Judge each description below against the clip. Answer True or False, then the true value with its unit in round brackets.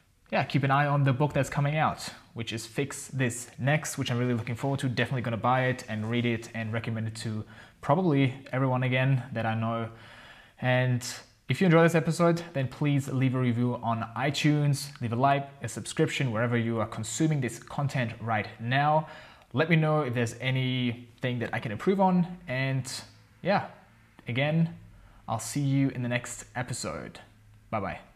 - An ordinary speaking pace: True (185 wpm)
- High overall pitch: False (125 Hz)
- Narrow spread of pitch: False (3.5 semitones)